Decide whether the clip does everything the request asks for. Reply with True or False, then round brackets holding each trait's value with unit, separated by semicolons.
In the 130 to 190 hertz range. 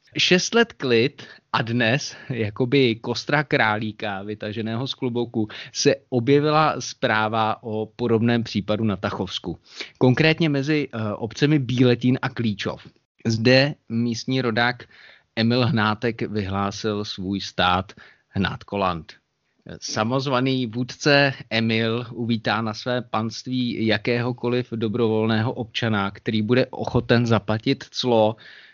False (115 Hz)